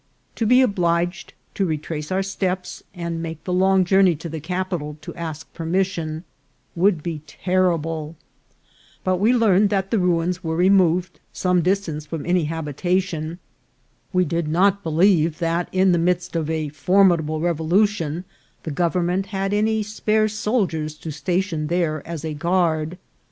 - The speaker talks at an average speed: Yes, average, 150 wpm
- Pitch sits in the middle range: Yes, medium, 175 Hz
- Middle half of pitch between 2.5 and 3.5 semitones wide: Yes, average, 2.9 semitones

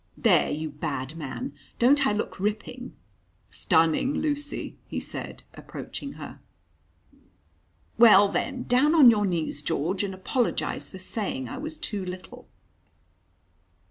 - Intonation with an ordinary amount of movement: No, wide, 7.3 semitones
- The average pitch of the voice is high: Yes, high, 210 Hz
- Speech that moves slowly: Yes, slow, 125 wpm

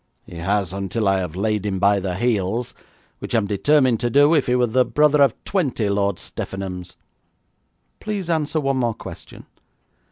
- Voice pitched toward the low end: Yes, low, 110 Hz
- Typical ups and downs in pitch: No, wide, 5.8 semitones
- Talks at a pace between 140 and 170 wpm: No, average, 180 wpm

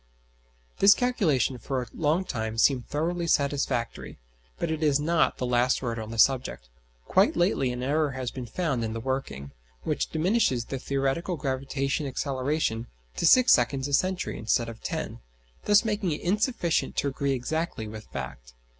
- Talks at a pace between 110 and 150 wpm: No, average, 165 wpm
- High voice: No, low, 135 Hz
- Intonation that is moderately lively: Yes, average, 4.9 semitones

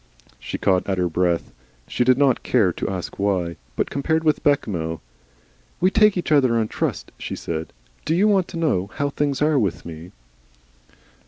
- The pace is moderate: Yes, average, 180 wpm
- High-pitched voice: No, low, 120 Hz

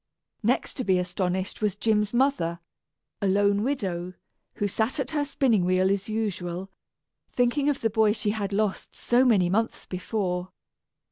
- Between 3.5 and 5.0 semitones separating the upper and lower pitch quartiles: Yes, average, 3.9 semitones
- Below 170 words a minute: Yes, average, 155 wpm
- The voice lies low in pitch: No, high, 205 Hz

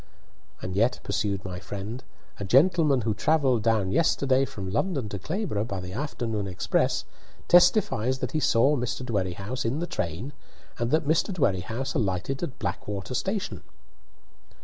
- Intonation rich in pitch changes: Yes, wide, 6.3 semitones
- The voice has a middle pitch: No, low, 120 Hz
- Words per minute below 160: Yes, average, 150 wpm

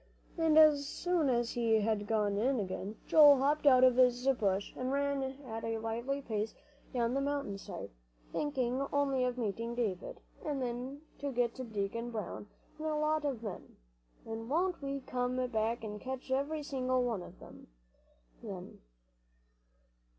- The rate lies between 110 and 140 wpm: No, average, 165 wpm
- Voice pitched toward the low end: No, very high, 250 Hz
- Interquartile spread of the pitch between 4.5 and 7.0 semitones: No, average, 3.9 semitones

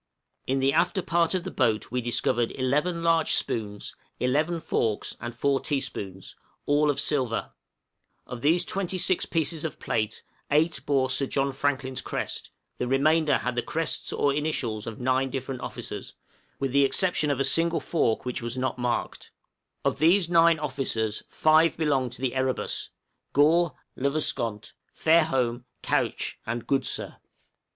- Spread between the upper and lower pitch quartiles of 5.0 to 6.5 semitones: No, average, 4.2 semitones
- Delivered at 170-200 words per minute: No, average, 155 wpm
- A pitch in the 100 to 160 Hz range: Yes, low, 135 Hz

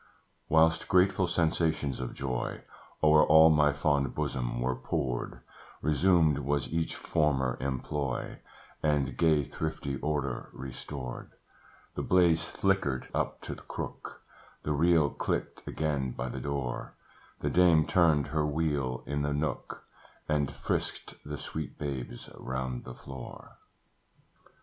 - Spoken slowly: Yes, slow, 125 wpm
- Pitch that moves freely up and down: No, average, 3.1 semitones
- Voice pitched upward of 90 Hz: No, very low, 75 Hz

